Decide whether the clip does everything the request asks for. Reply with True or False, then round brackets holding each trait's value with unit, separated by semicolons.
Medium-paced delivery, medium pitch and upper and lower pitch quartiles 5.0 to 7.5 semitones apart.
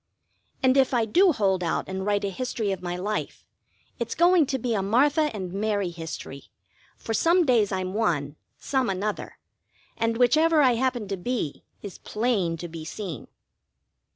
False (170 wpm; 215 Hz; 5.3 semitones)